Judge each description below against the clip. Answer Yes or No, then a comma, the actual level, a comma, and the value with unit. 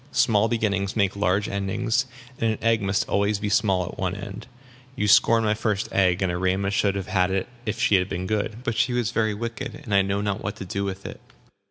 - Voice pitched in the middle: No, low, 100 Hz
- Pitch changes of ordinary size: No, narrow, 2.1 semitones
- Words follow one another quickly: Yes, fast, 230 wpm